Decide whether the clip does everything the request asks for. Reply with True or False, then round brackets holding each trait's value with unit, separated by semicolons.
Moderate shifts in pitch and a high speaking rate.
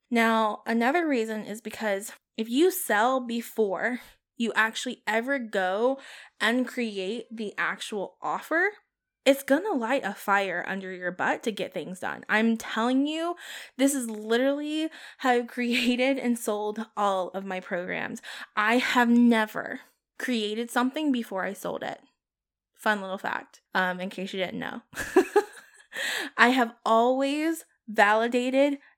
False (4.0 semitones; 140 wpm)